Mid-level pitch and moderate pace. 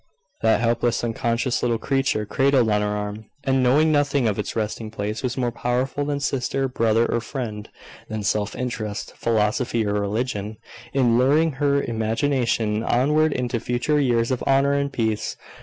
No: low, 120 Hz; average, 160 wpm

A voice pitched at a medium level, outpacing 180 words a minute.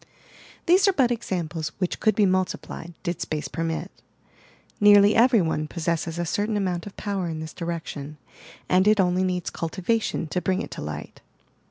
No: medium, 180 Hz; average, 170 wpm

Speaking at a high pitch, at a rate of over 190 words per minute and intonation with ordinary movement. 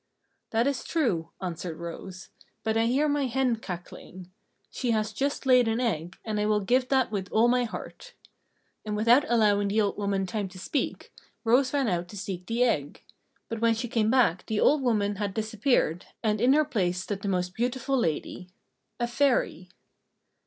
No: high, 220 Hz; average, 185 wpm; average, 4.5 semitones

